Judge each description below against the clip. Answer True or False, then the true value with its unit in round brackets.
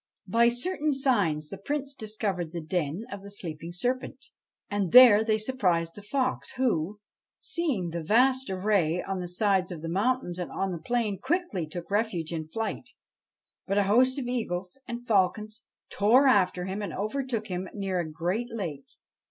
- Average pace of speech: True (175 wpm)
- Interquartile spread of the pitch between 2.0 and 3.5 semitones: False (5.3 semitones)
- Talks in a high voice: True (205 Hz)